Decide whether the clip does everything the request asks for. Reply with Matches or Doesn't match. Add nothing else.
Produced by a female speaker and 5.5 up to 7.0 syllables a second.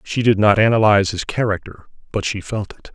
Doesn't match